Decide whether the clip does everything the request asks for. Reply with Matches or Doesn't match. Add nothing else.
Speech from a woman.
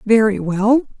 Matches